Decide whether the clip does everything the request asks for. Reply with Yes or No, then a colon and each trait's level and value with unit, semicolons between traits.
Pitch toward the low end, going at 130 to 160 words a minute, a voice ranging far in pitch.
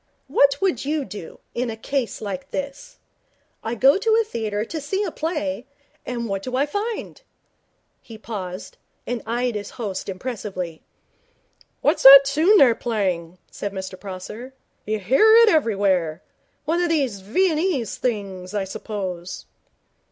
No: high, 235 Hz; average, 145 wpm; wide, 6.3 semitones